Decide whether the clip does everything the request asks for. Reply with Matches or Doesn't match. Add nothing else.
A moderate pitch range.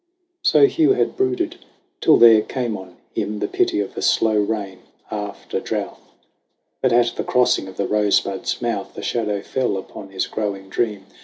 Matches